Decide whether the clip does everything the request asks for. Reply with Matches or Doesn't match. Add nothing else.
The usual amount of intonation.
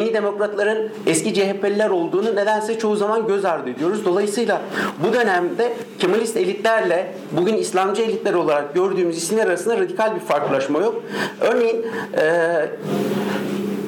Doesn't match